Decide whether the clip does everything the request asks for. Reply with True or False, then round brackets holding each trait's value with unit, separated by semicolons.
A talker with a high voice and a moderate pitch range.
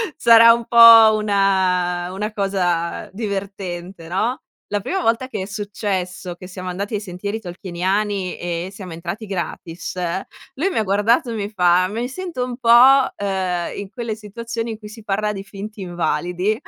True (200 Hz; 3.4 semitones)